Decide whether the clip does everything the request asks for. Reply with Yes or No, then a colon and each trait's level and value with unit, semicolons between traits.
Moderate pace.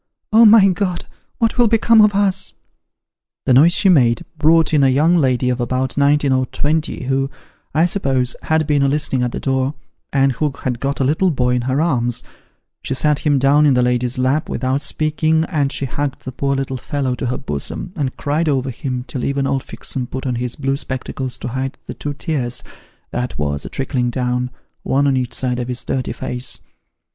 No: fast, 210 wpm